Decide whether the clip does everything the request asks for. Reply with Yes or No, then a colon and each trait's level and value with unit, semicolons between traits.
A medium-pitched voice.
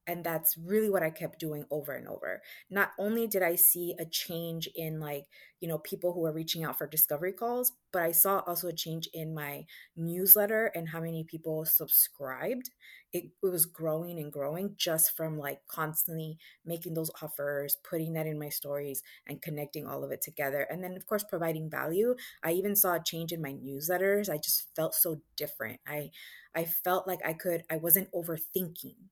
Yes: medium, 165 Hz